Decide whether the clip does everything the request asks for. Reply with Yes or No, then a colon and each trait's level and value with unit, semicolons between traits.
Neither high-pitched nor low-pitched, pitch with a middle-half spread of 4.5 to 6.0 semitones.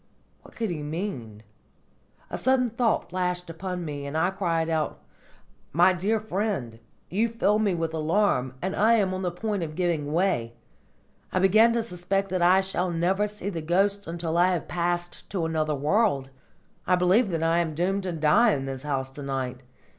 No: medium, 175 Hz; average, 4.0 semitones